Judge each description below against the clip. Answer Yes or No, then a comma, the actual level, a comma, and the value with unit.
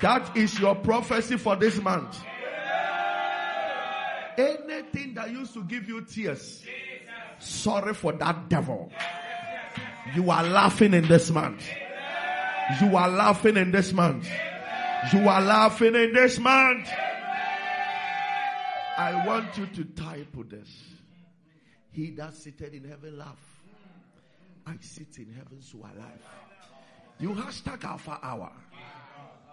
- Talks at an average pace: No, slow, 130 wpm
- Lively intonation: Yes, wide, 6.9 semitones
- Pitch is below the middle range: No, high, 195 Hz